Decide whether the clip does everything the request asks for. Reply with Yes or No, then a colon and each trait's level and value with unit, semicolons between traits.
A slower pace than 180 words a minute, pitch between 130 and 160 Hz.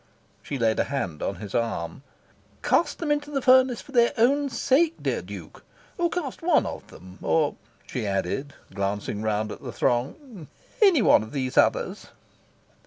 Yes: average, 170 wpm; medium, 140 Hz